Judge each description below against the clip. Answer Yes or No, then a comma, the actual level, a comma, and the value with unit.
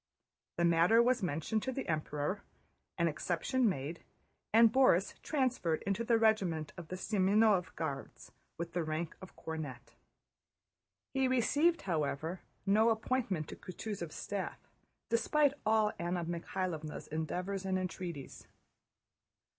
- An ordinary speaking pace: No, slow, 120 wpm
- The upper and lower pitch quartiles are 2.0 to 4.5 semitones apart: No, wide, 5.5 semitones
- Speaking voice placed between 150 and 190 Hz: Yes, medium, 185 Hz